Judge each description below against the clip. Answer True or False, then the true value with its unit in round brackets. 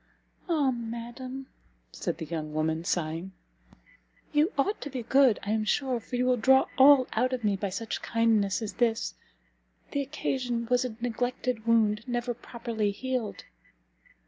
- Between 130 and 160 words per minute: True (155 wpm)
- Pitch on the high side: True (235 Hz)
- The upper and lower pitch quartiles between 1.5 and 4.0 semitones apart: True (3.3 semitones)